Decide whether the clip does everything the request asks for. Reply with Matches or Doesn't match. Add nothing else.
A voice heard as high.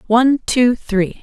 Matches